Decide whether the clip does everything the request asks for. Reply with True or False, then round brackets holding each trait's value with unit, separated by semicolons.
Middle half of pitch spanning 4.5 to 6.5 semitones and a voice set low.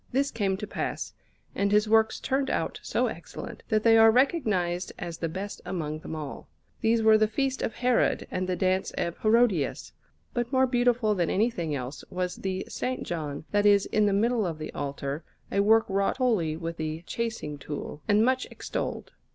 False (5.1 semitones; 200 Hz)